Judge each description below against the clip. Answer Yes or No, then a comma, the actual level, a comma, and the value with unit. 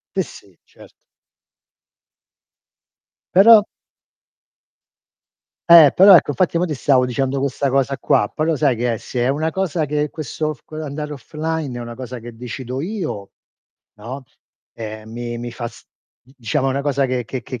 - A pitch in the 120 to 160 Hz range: Yes, low, 135 Hz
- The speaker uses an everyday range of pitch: Yes, average, 4.1 semitones